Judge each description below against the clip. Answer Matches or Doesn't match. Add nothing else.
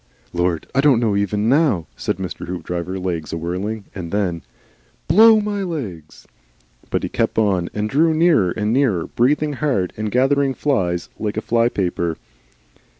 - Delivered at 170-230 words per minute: Doesn't match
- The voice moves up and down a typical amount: Doesn't match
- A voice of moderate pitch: Doesn't match